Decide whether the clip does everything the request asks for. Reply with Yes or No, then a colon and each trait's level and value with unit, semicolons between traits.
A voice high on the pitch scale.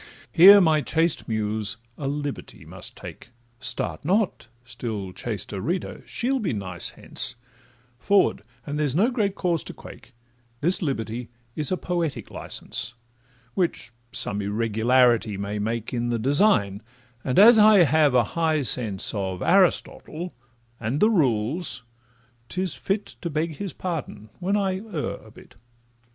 No: medium, 145 Hz